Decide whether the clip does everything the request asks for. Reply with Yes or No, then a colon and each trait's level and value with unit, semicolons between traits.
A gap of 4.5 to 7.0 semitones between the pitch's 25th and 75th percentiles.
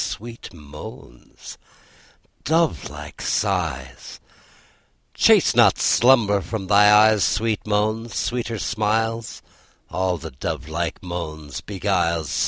Yes: average, 4.9 semitones